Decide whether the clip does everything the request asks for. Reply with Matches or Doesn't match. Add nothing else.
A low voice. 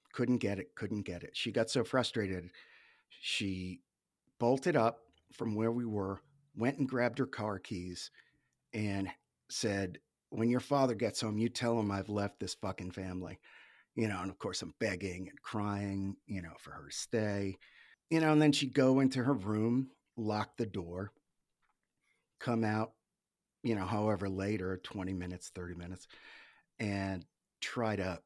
Matches